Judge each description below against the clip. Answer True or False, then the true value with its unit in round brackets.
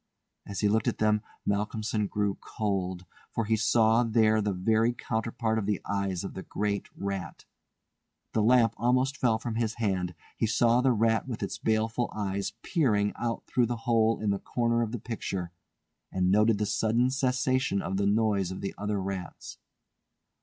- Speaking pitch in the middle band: False (110 Hz)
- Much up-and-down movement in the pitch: False (2.5 semitones)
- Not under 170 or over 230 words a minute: True (175 wpm)